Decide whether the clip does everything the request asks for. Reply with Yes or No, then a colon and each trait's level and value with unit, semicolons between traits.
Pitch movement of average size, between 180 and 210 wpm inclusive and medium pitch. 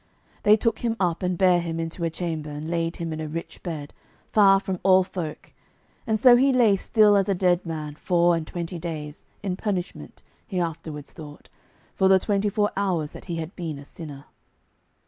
Yes: average, 3.3 semitones; average, 200 wpm; medium, 175 Hz